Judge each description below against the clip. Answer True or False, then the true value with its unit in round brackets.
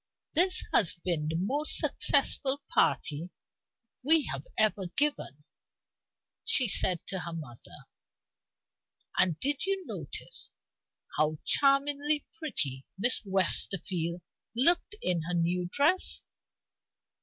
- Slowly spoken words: True (105 wpm)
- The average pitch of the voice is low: False (195 Hz)